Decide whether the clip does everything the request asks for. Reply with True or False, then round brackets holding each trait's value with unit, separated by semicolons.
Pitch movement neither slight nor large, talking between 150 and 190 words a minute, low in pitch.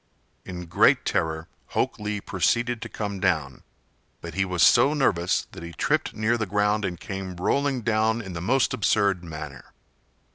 True (4.3 semitones; 170 wpm; 100 Hz)